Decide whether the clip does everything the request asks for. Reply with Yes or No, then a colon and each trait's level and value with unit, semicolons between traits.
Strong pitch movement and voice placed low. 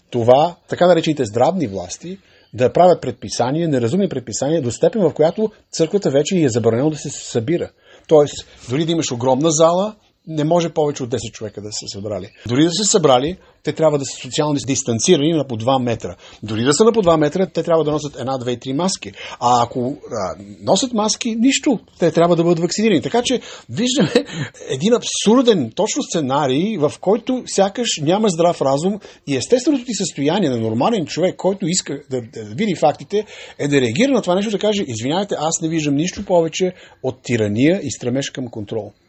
No: wide, 6.6 semitones; medium, 155 Hz